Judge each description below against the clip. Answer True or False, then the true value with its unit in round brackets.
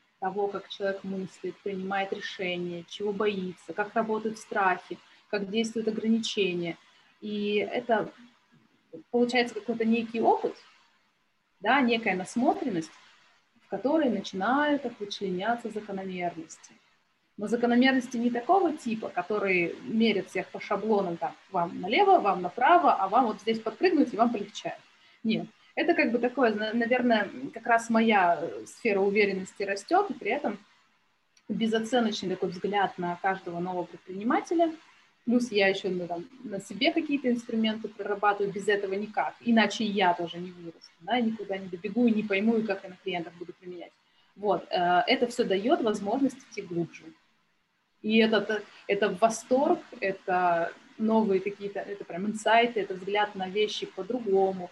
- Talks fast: False (140 wpm)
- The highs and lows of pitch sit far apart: False (3.7 semitones)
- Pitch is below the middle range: False (210 Hz)